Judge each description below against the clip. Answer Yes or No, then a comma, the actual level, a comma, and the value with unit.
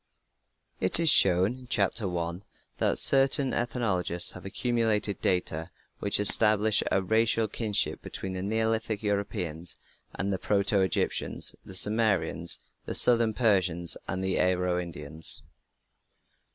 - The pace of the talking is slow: Yes, slow, 115 wpm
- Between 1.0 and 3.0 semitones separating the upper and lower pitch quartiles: No, average, 3.5 semitones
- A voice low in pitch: Yes, low, 100 Hz